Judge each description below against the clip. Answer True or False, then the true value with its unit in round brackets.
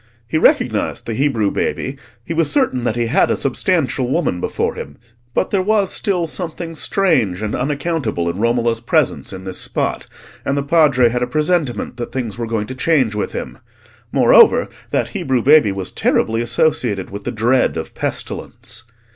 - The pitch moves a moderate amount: False (5.9 semitones)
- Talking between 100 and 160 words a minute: False (175 wpm)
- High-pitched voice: False (125 Hz)